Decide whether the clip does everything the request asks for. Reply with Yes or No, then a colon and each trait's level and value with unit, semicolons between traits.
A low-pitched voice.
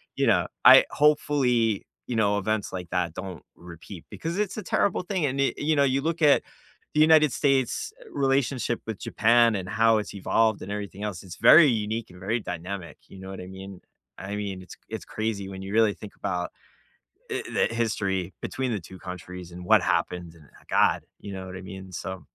Yes: low, 105 Hz